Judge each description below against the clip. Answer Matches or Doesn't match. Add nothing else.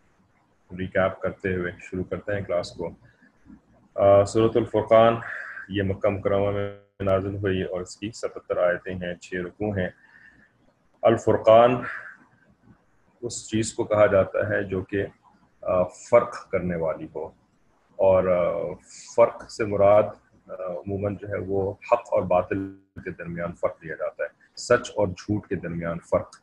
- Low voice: Matches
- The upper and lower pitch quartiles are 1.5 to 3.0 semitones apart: Matches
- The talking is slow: Doesn't match